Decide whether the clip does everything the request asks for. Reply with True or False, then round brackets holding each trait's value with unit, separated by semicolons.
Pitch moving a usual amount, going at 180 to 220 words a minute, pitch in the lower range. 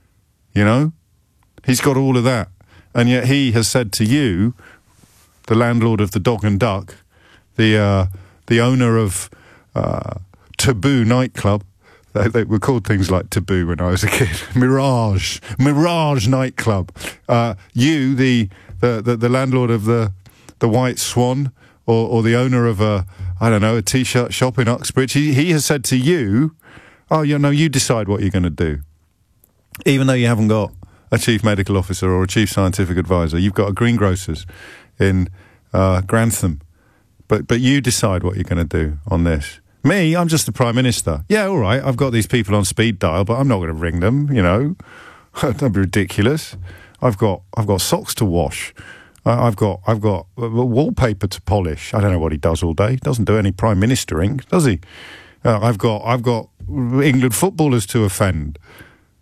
True (4.8 semitones; 190 wpm; 110 Hz)